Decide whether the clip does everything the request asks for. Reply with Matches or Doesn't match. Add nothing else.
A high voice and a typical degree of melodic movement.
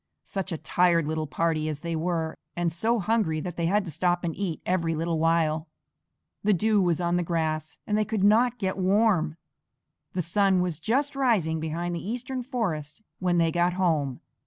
Doesn't match